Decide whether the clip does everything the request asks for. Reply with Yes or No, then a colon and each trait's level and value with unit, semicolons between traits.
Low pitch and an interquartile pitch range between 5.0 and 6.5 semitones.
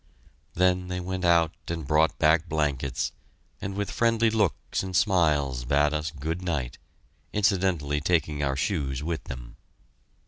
No: very low, 80 Hz; average, 4.1 semitones